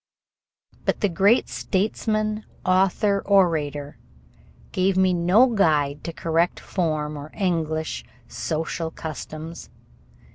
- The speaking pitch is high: No, medium, 170 Hz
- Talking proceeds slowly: Yes, slow, 100 wpm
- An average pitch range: Yes, average, 3.9 semitones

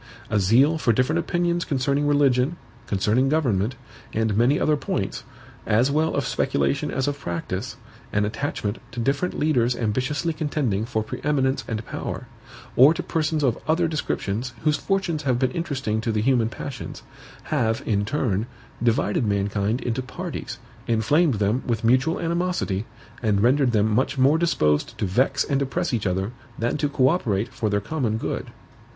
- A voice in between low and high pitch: No, low, 130 Hz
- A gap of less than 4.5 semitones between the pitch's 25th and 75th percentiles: No, average, 5.1 semitones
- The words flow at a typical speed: Yes, average, 165 wpm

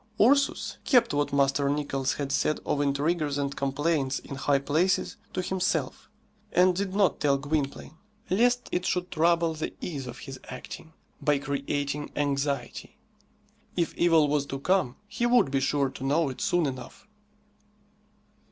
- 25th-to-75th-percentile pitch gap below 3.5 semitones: No, average, 4.0 semitones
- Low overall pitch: No, medium, 145 Hz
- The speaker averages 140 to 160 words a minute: Yes, average, 150 wpm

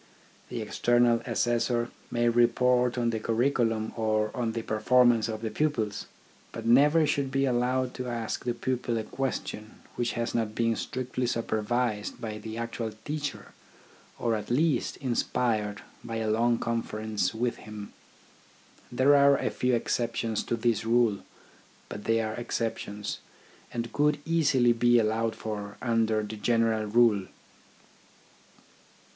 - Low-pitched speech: Yes, low, 115 Hz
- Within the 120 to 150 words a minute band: Yes, average, 140 wpm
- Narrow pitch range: Yes, narrow, 2.1 semitones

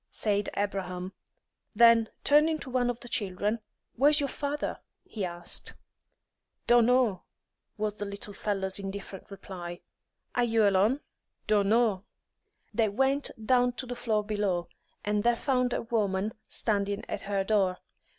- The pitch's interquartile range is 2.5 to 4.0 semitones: Yes, average, 3.6 semitones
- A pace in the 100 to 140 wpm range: Yes, slow, 135 wpm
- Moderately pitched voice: No, high, 210 Hz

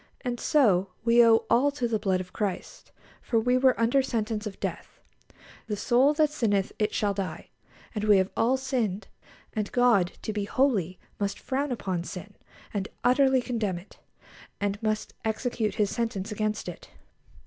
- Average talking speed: Yes, average, 170 wpm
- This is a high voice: Yes, high, 220 Hz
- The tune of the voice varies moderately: Yes, average, 3.6 semitones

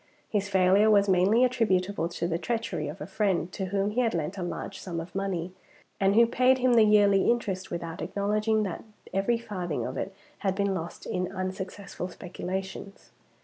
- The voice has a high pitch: Yes, high, 195 Hz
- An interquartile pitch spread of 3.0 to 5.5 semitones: No, narrow, 2.5 semitones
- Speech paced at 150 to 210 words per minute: Yes, average, 185 wpm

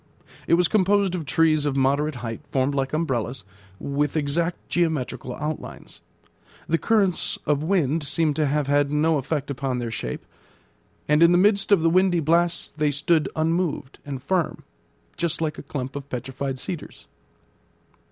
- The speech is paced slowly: No, average, 160 wpm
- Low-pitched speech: No, medium, 150 Hz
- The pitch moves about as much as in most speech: Yes, average, 3.3 semitones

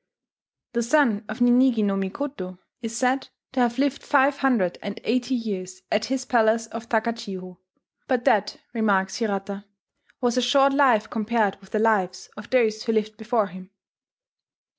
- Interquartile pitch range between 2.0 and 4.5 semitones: Yes, average, 3.6 semitones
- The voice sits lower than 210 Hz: No, high, 225 Hz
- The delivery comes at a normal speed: Yes, average, 160 wpm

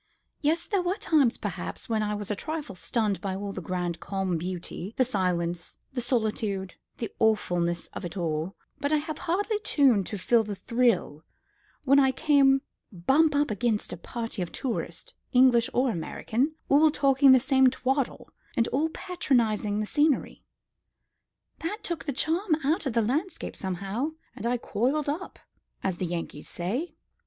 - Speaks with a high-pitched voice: Yes, high, 240 Hz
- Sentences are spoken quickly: No, average, 165 wpm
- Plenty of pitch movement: Yes, wide, 6.9 semitones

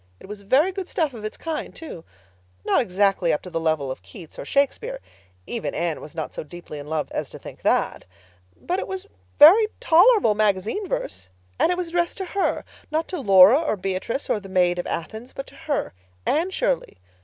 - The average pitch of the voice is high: Yes, high, 220 Hz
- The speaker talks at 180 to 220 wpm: Yes, average, 200 wpm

